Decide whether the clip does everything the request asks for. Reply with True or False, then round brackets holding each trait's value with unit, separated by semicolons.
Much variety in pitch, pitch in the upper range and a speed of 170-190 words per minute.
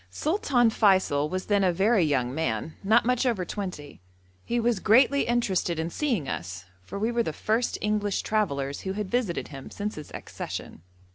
True (6.9 semitones; 200 Hz; 180 wpm)